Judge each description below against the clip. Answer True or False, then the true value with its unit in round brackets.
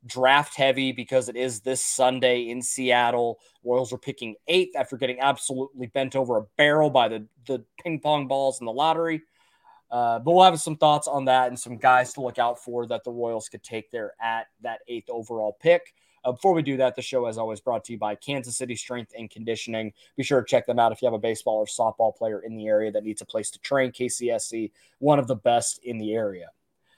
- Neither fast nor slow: False (230 wpm)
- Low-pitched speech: True (125 Hz)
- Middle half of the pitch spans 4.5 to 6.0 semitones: False (2.9 semitones)